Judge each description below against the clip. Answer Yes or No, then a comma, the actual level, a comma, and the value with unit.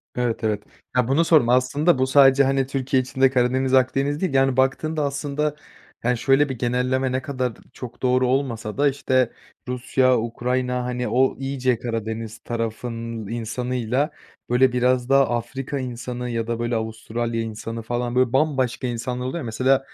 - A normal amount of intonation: No, narrow, 2.1 semitones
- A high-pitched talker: No, low, 125 Hz